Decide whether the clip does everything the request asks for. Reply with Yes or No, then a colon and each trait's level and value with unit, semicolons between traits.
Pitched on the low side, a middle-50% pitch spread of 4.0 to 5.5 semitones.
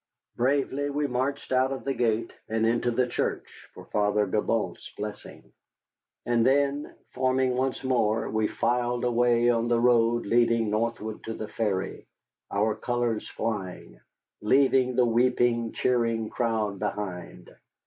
No: low, 120 Hz; narrow, 2.4 semitones